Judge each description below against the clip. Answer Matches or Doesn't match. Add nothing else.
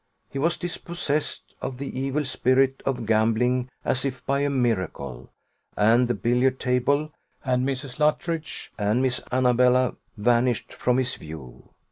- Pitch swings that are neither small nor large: Doesn't match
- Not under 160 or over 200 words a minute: Doesn't match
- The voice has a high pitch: Doesn't match